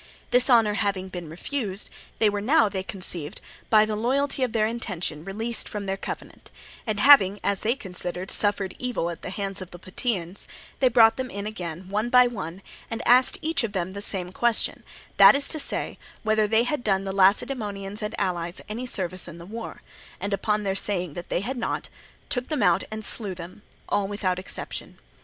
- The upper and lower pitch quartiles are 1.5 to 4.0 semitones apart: Yes, average, 3.7 semitones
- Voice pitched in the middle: No, high, 205 Hz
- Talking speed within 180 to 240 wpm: Yes, average, 195 wpm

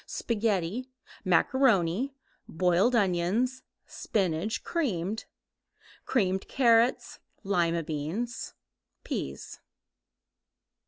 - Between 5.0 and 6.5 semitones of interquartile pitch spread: Yes, wide, 5.6 semitones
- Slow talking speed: Yes, slow, 60 wpm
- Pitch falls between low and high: No, high, 200 Hz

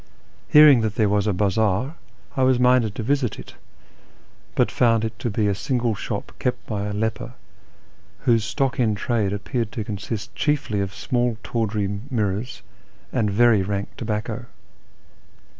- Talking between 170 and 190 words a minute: No, average, 155 wpm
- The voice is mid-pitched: No, low, 110 Hz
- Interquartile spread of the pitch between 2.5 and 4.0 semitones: Yes, average, 3.1 semitones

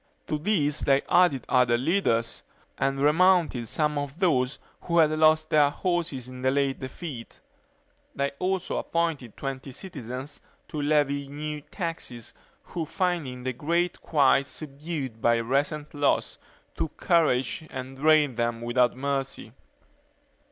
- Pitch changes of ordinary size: Yes, average, 3.5 semitones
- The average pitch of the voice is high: No, medium, 145 Hz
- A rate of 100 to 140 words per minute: Yes, slow, 135 wpm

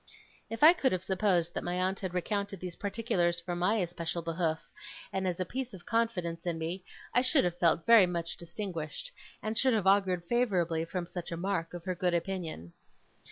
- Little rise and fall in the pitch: No, average, 3.0 semitones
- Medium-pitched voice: Yes, medium, 180 Hz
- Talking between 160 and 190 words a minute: No, average, 200 wpm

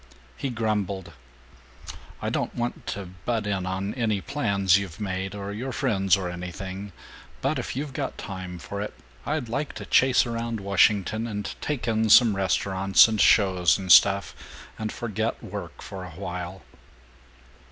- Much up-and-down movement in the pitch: No, average, 3.2 semitones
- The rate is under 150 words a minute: No, average, 155 wpm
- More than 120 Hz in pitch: No, low, 100 Hz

